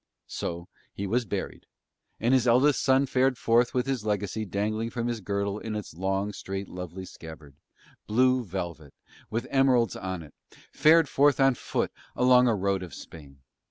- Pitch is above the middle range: No, low, 110 Hz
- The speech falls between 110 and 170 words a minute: Yes, average, 165 wpm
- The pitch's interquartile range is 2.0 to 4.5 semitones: No, average, 5.0 semitones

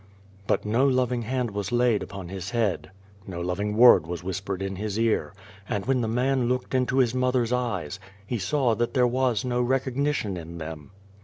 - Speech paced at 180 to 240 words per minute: Yes, average, 190 wpm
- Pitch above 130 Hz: No, low, 115 Hz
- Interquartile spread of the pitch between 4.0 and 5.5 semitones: Yes, average, 4.7 semitones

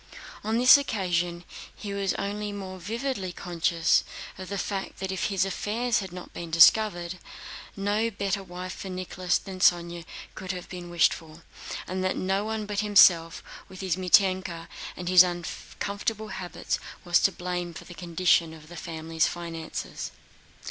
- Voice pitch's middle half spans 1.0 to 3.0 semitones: Yes, narrow, 2.6 semitones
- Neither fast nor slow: Yes, average, 160 wpm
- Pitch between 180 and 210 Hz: Yes, medium, 185 Hz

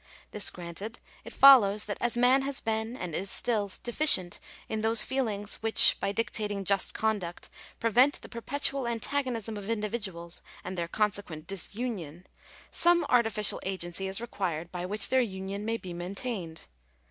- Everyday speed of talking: Yes, average, 155 wpm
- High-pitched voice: Yes, high, 210 Hz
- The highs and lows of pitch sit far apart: No, average, 3.8 semitones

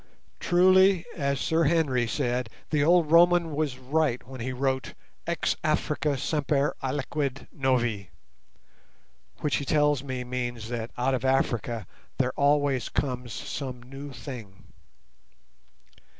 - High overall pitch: No, low, 135 Hz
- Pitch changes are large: No, average, 3.1 semitones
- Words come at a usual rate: No, slow, 120 wpm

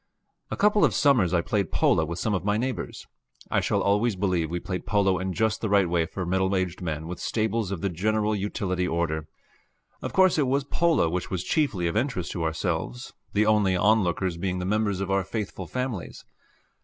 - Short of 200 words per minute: No, fast, 205 wpm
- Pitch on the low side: Yes, very low, 95 Hz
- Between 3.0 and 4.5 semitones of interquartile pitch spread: Yes, average, 3.5 semitones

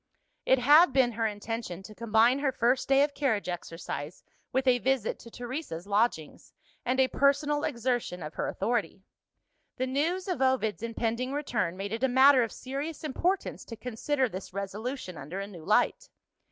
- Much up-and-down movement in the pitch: No, average, 4.6 semitones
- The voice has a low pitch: No, high, 245 Hz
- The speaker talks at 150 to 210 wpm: Yes, average, 170 wpm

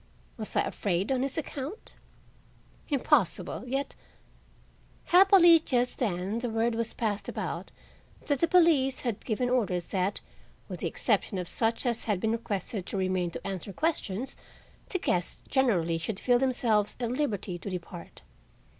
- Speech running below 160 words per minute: Yes, average, 150 wpm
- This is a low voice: No, high, 230 Hz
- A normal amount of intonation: No, wide, 5.7 semitones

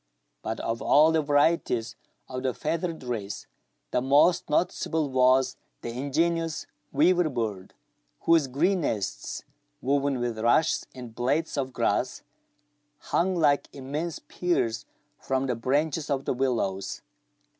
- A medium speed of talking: No, slow, 125 wpm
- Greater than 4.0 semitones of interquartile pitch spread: Yes, average, 4.4 semitones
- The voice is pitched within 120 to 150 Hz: Yes, low, 135 Hz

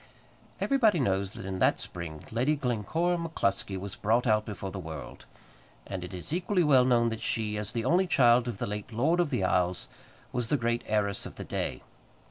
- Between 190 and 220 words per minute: Yes, average, 200 wpm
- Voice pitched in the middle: No, low, 115 Hz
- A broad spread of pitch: Yes, wide, 5.9 semitones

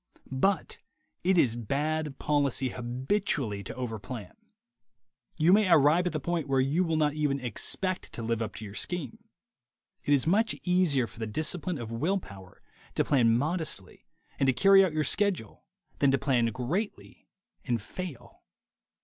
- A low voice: No, medium, 145 Hz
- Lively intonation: Yes, wide, 6.6 semitones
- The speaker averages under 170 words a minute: Yes, average, 160 wpm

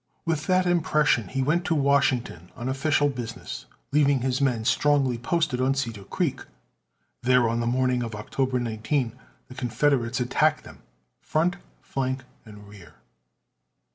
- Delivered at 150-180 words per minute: No, average, 140 wpm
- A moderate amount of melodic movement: Yes, average, 3.6 semitones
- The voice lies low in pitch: Yes, low, 130 Hz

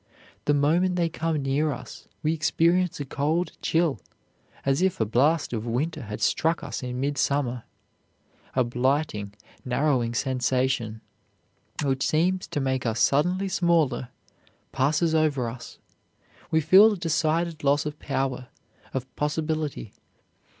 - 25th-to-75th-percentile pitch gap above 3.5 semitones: Yes, average, 4.2 semitones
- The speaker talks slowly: Yes, slow, 130 wpm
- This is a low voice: No, medium, 145 Hz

